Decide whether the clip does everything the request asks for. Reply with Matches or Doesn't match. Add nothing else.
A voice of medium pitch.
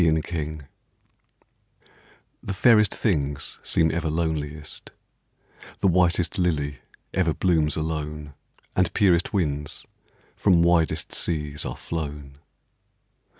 Doesn't match